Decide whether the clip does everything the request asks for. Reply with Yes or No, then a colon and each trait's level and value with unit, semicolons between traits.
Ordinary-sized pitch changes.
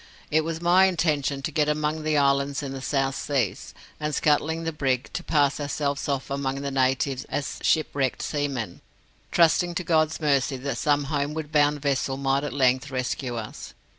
No: narrow, 2.1 semitones